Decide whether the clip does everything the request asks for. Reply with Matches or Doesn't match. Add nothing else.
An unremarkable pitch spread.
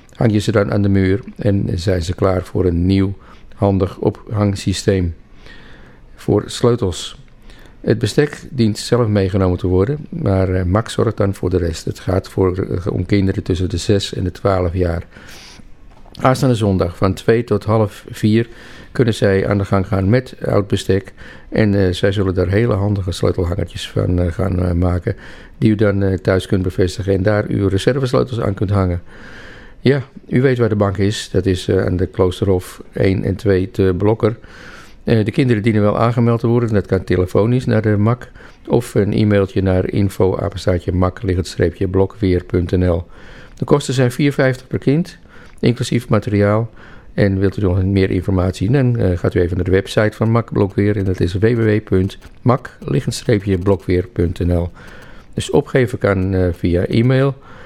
Matches